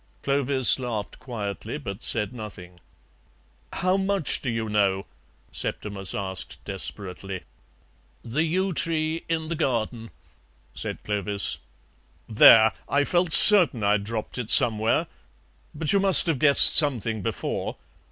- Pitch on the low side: Yes, low, 120 Hz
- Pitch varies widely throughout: Yes, wide, 7.0 semitones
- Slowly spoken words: Yes, slow, 125 wpm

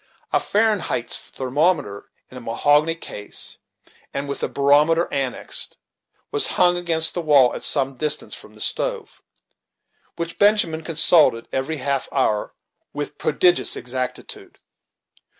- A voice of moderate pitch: Yes, medium, 145 Hz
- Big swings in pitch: No, average, 4.1 semitones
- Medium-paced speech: No, slow, 130 wpm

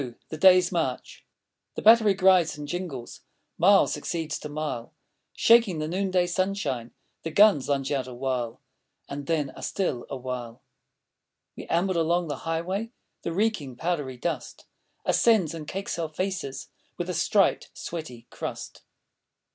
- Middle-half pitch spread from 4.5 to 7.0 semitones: Yes, average, 5.2 semitones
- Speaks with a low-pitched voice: No, medium, 165 Hz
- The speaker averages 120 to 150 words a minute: Yes, average, 140 wpm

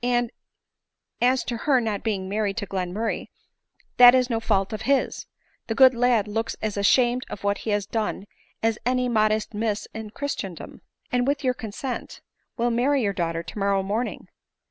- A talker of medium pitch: No, high, 225 Hz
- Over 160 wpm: Yes, average, 170 wpm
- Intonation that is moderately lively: Yes, average, 3.4 semitones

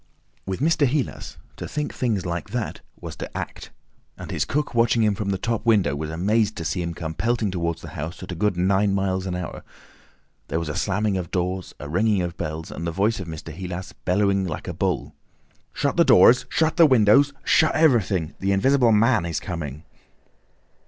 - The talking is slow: No, average, 200 wpm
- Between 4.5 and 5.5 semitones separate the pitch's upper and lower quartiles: Yes, average, 4.9 semitones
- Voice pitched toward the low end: Yes, very low, 95 Hz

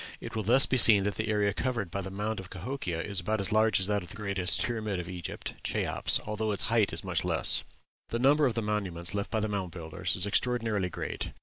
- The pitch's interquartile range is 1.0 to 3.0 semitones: Yes, average, 2.7 semitones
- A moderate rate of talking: No, fast, 235 wpm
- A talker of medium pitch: No, low, 105 Hz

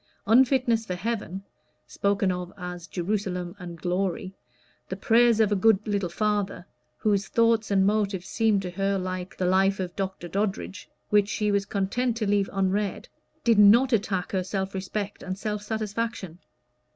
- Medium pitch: No, high, 200 Hz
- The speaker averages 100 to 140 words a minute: No, average, 160 wpm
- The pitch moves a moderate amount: No, narrow, 2.3 semitones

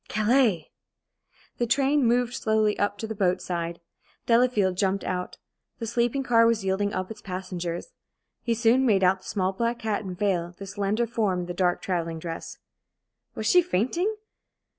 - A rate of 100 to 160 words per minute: No, average, 170 wpm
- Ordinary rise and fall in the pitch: Yes, average, 4.2 semitones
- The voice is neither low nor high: No, high, 205 Hz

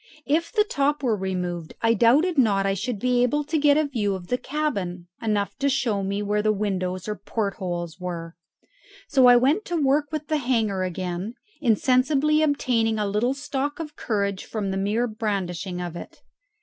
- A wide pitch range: Yes, wide, 6.3 semitones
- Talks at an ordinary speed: Yes, average, 190 wpm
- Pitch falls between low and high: No, high, 225 Hz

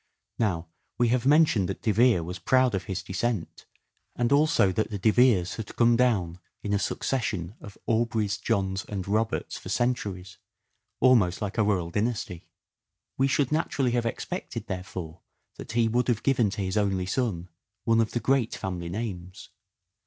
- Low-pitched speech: Yes, low, 105 Hz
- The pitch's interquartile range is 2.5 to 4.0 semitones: No, average, 4.4 semitones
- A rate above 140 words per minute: Yes, average, 175 wpm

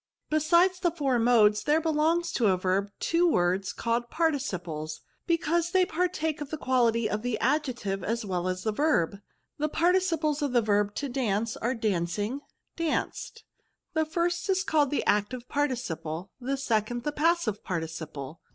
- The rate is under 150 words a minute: No, average, 175 wpm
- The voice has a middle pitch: No, very high, 250 Hz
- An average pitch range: No, wide, 7.5 semitones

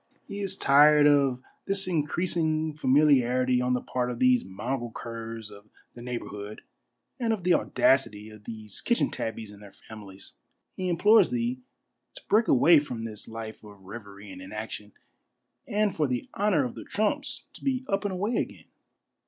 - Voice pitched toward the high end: No, low, 130 Hz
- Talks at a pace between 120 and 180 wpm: Yes, average, 170 wpm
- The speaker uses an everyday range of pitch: No, wide, 8.5 semitones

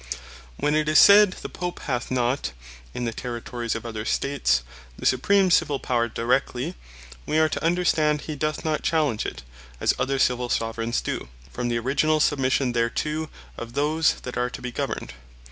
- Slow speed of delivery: No, average, 175 wpm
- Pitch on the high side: No, low, 130 Hz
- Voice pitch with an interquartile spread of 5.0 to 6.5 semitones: No, average, 4.4 semitones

